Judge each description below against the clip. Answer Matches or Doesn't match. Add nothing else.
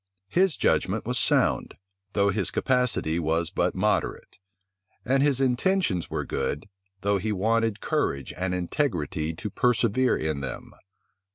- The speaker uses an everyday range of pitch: Doesn't match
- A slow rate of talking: Matches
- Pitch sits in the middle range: Doesn't match